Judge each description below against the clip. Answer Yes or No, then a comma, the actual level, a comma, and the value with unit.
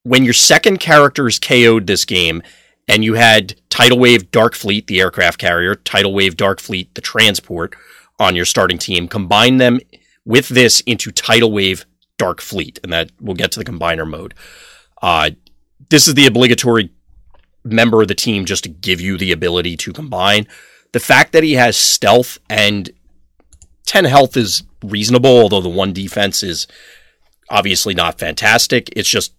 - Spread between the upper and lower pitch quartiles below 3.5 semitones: No, average, 5.0 semitones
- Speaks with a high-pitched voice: No, low, 105 Hz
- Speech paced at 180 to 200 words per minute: No, average, 170 wpm